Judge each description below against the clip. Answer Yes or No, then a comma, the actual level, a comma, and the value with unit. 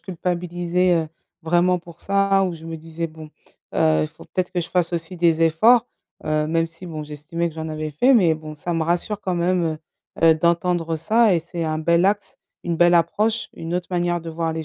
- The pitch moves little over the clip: Yes, narrow, 1.9 semitones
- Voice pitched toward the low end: No, medium, 170 Hz